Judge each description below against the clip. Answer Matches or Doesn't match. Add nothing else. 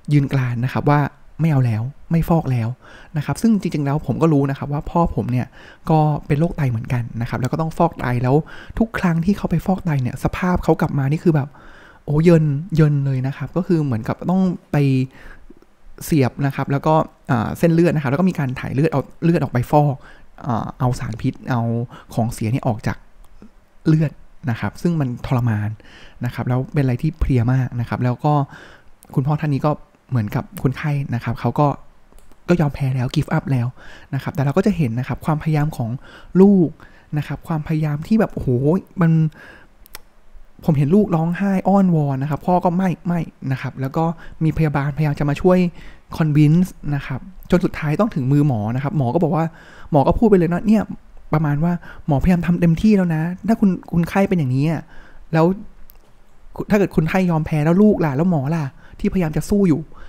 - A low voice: Doesn't match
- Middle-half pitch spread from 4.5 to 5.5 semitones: Doesn't match